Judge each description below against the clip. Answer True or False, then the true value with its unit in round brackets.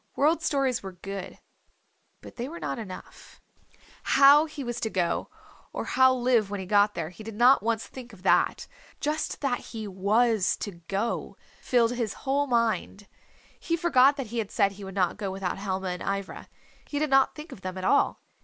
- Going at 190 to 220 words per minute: True (195 wpm)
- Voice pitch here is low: False (225 Hz)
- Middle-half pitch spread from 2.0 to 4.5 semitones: False (5.3 semitones)